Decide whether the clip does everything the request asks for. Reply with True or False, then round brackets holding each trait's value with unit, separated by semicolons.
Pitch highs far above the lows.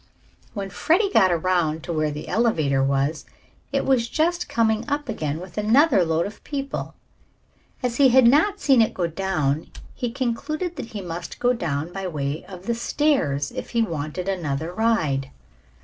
True (7.6 semitones)